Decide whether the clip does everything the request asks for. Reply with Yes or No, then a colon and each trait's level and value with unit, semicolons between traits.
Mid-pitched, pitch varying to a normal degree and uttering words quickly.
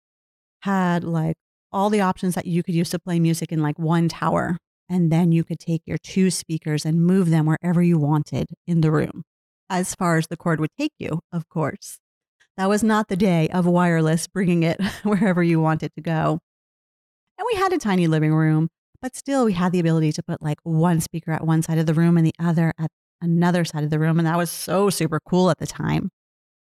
No: medium, 170 Hz; narrow, 2.1 semitones; fast, 220 wpm